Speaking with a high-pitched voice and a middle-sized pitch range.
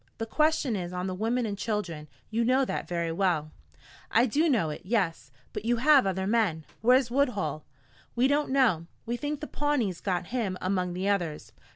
No: high, 210 Hz; wide, 5.9 semitones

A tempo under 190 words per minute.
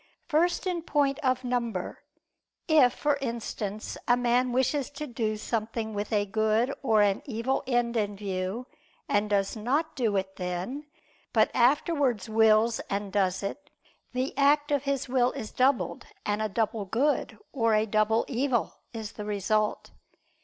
Yes: average, 155 wpm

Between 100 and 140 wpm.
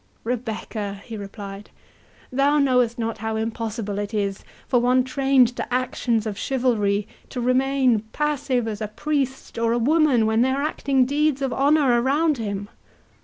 No: average, 160 wpm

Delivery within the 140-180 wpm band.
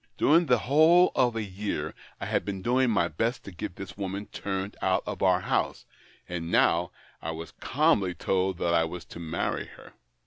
No: average, 200 wpm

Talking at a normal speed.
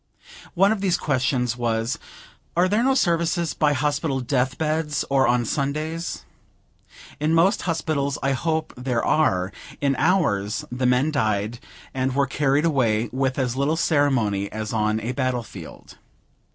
Yes: average, 150 wpm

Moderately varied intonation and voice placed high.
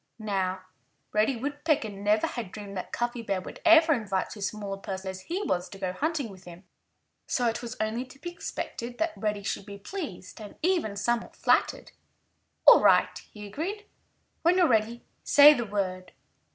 No: wide, 6.3 semitones; high, 220 Hz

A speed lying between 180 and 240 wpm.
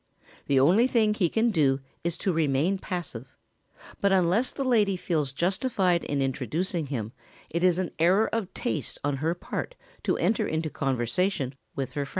No: average, 170 wpm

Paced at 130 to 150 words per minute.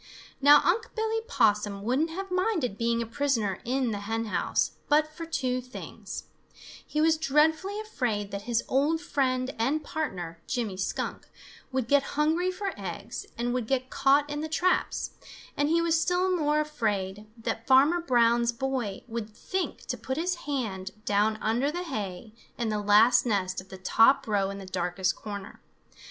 No: average, 170 wpm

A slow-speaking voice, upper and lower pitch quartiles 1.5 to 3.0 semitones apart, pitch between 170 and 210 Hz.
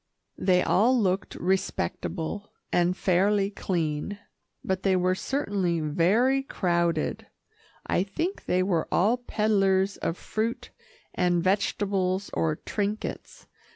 Yes: slow, 110 wpm; average, 2.7 semitones; high, 190 Hz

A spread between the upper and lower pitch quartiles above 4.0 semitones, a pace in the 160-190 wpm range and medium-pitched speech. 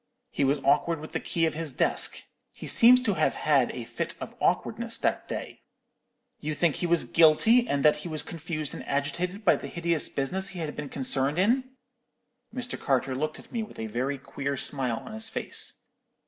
No: average, 4.5 semitones; fast, 205 wpm; medium, 155 Hz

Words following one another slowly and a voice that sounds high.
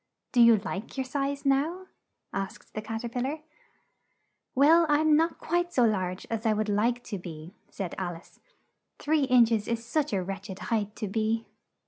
No: average, 190 wpm; high, 230 Hz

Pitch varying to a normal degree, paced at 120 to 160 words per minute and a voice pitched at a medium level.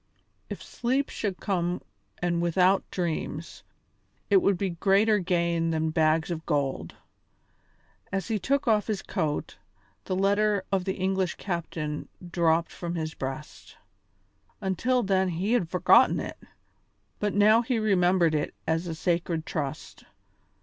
Yes: average, 3.4 semitones; slow, 135 wpm; medium, 180 Hz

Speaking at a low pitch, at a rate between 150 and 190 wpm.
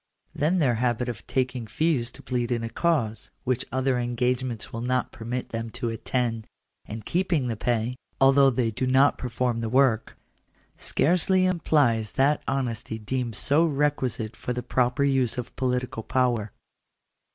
Yes: low, 125 Hz; average, 155 wpm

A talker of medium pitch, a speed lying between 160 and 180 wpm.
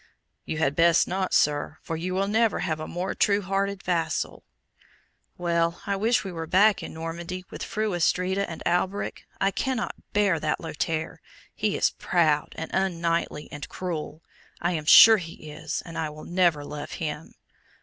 Yes: medium, 170 Hz; average, 170 wpm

